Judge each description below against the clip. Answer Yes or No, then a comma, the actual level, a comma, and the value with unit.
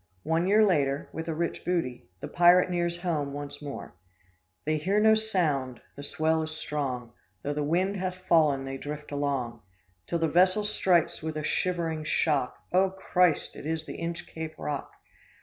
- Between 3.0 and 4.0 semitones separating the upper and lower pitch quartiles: Yes, average, 3.7 semitones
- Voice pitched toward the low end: No, medium, 160 Hz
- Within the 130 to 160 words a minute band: No, average, 170 wpm